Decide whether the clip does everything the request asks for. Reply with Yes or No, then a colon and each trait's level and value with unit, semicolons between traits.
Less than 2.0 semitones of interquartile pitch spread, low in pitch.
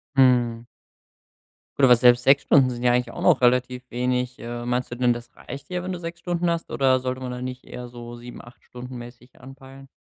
Yes: narrow, 1.6 semitones; low, 125 Hz